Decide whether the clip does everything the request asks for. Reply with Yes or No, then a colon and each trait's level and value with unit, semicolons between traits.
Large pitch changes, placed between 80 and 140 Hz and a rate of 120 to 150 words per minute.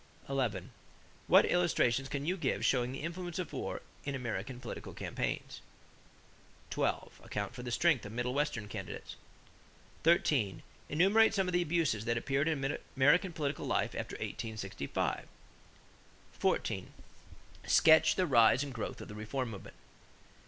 Yes: wide, 5.9 semitones; low, 135 Hz; average, 140 wpm